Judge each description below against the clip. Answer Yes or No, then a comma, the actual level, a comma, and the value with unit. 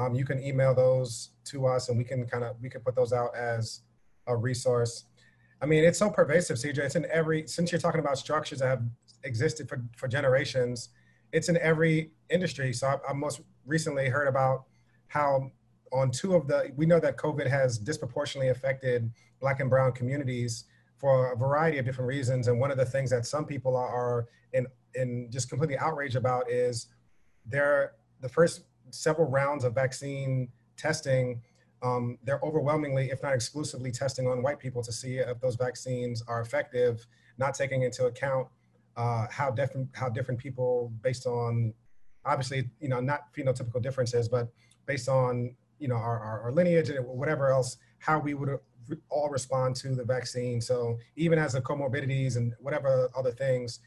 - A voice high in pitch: No, low, 130 Hz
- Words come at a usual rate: Yes, average, 180 wpm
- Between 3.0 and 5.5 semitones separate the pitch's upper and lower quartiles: No, narrow, 2.6 semitones